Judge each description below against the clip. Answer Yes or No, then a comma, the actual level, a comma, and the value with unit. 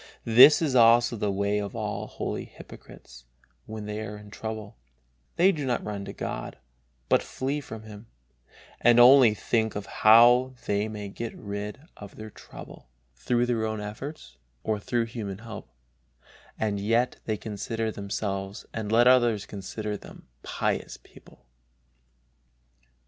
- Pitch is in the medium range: No, low, 110 Hz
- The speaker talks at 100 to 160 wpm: Yes, average, 145 wpm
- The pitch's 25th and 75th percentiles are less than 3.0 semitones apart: Yes, narrow, 2.6 semitones